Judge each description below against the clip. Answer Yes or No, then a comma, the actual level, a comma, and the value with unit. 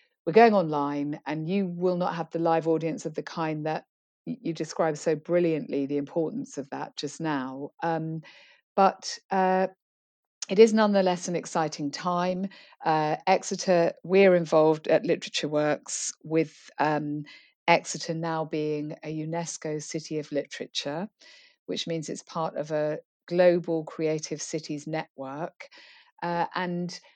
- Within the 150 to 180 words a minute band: No, average, 140 wpm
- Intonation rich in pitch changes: No, average, 2.8 semitones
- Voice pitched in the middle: Yes, medium, 165 Hz